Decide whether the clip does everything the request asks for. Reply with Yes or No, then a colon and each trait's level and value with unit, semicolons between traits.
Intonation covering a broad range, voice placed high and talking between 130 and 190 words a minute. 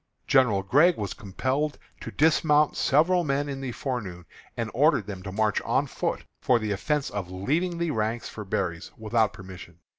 No: wide, 6.7 semitones; low, 120 Hz; average, 175 wpm